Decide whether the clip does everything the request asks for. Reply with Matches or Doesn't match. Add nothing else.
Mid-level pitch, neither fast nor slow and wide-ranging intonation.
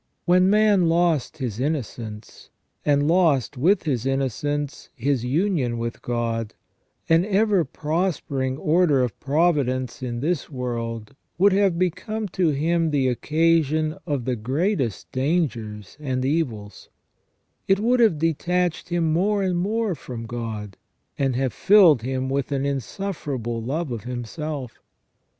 Doesn't match